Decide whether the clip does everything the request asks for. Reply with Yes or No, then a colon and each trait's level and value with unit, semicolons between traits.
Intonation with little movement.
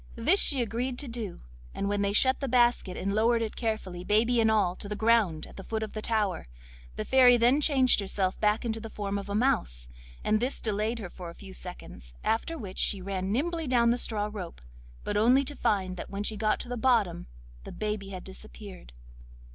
No: average, 3.4 semitones